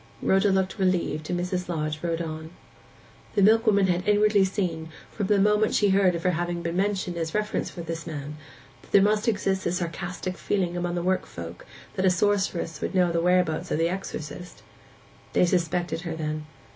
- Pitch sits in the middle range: Yes, medium, 180 Hz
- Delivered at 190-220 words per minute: Yes, average, 195 wpm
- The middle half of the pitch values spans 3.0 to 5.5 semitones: No, narrow, 2.6 semitones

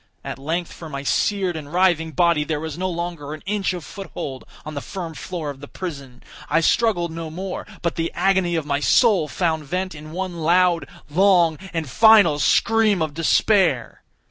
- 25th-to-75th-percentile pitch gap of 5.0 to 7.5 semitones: No, average, 3.5 semitones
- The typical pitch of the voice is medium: Yes, medium, 170 Hz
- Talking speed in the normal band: Yes, average, 185 wpm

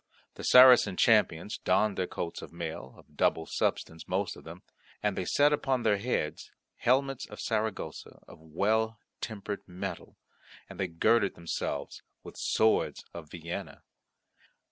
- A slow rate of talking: No, average, 145 wpm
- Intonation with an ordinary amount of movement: Yes, average, 4.7 semitones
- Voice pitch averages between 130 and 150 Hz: No, low, 100 Hz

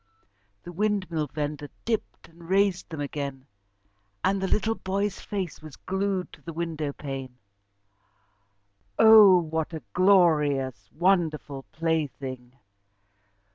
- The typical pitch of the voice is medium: Yes, medium, 165 Hz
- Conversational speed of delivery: No, slow, 110 wpm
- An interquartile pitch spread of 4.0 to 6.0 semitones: Yes, average, 4.8 semitones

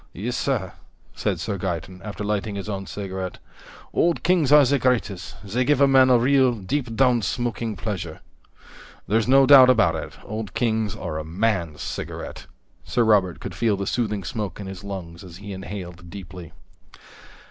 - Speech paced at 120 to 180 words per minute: Yes, average, 170 wpm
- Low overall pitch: Yes, low, 105 Hz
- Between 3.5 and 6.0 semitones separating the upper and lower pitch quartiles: Yes, average, 4.6 semitones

